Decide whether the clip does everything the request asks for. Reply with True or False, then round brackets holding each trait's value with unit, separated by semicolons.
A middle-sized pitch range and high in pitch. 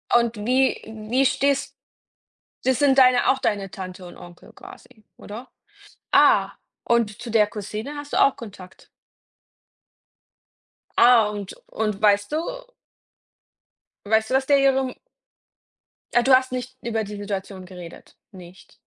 True (4.2 semitones; 225 Hz)